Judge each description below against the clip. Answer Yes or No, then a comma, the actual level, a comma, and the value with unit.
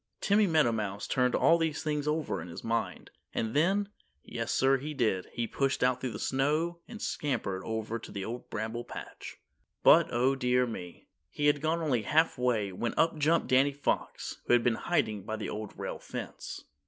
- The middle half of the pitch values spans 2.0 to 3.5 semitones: No, average, 5.2 semitones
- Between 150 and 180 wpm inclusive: No, average, 190 wpm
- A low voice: Yes, low, 125 Hz